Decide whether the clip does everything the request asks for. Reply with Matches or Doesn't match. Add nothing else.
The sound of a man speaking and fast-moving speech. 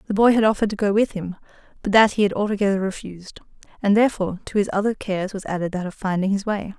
Doesn't match